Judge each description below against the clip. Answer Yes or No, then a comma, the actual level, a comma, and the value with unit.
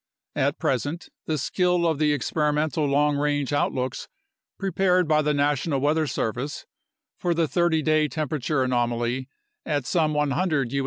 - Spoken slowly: No, average, 145 wpm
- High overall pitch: No, medium, 150 Hz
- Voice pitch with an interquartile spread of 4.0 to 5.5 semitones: No, narrow, 2.4 semitones